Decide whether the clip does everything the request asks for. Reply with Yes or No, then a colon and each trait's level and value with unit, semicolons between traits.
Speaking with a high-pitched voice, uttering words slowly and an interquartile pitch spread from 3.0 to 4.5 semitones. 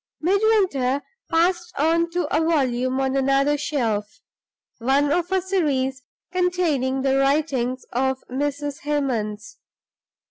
Yes: very high, 280 Hz; slow, 110 wpm; average, 4.2 semitones